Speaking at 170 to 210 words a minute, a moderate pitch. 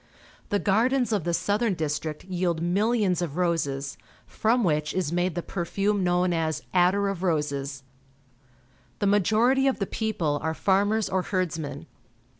No: average, 145 wpm; medium, 180 Hz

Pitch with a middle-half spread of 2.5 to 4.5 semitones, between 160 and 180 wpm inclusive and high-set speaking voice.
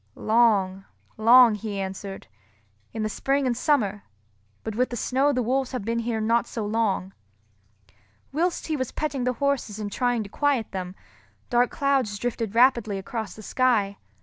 Yes: average, 3.7 semitones; average, 165 wpm; high, 230 Hz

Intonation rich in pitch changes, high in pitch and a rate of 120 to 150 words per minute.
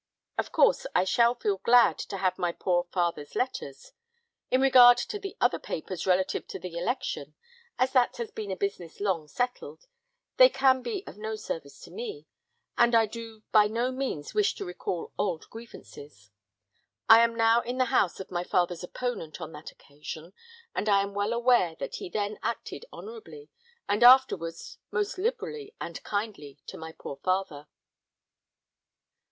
No: wide, 5.9 semitones; high, 215 Hz; average, 170 wpm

